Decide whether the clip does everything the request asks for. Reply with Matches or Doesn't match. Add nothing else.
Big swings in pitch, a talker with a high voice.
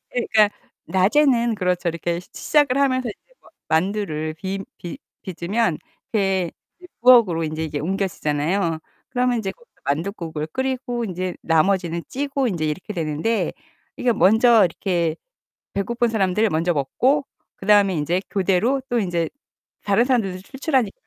Matches